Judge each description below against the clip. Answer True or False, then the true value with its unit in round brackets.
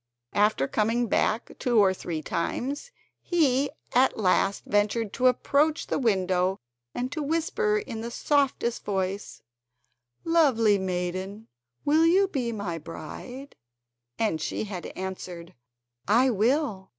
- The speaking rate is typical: False (125 wpm)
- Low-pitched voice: False (225 Hz)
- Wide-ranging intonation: True (6.6 semitones)